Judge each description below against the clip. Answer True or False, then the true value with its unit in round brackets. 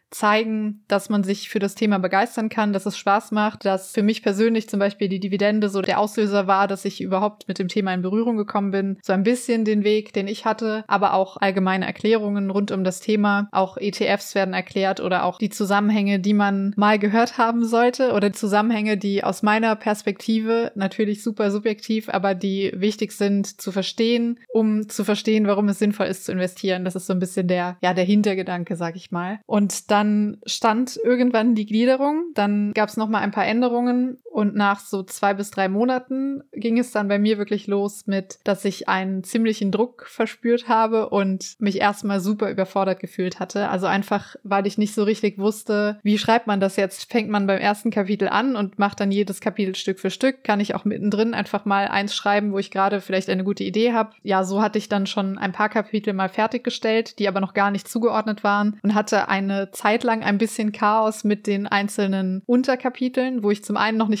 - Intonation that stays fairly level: True (1.8 semitones)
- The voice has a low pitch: False (205 Hz)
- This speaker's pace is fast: True (210 wpm)